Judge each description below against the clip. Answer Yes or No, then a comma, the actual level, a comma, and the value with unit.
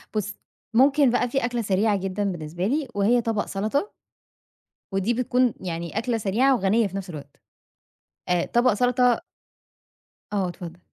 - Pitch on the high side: Yes, high, 215 Hz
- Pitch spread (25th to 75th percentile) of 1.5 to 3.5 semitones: No, average, 4.5 semitones